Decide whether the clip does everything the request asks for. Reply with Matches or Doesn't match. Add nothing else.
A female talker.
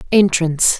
Matches